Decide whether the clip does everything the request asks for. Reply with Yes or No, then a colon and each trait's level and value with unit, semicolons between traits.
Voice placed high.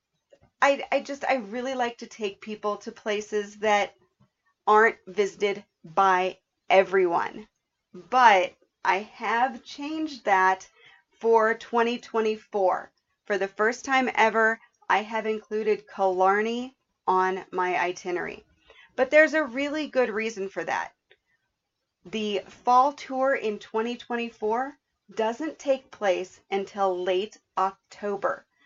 Yes: high, 215 Hz